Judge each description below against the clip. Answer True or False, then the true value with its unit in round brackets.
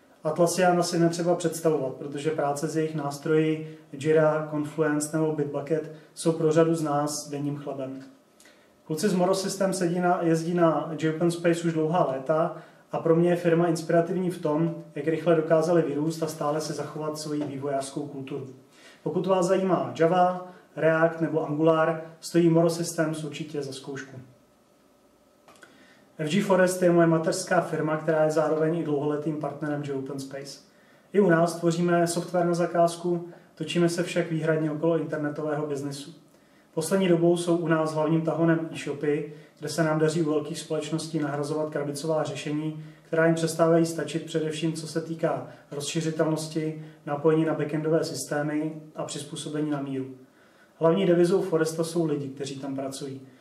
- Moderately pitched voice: True (160 Hz)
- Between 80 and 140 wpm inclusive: False (155 wpm)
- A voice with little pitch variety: True (1.9 semitones)